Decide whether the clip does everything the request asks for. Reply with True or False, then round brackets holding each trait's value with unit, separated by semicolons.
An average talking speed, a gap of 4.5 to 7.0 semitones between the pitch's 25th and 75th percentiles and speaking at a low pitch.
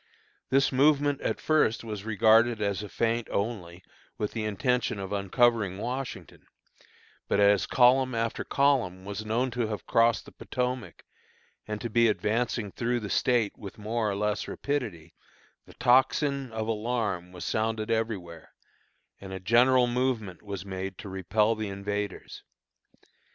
False (145 wpm; 3.3 semitones; 110 Hz)